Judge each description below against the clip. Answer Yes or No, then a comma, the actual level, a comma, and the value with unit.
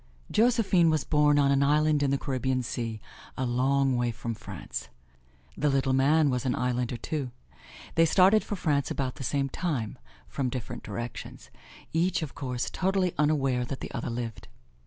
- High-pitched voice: No, low, 135 Hz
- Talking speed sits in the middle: Yes, average, 170 wpm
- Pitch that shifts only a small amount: No, average, 3.6 semitones